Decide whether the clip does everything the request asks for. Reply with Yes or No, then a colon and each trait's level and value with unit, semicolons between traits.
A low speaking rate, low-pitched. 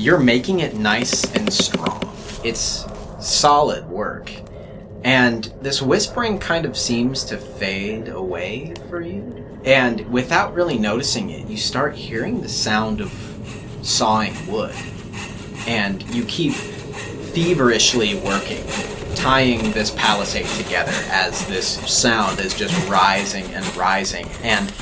Yes: slow, 125 wpm; low, 110 Hz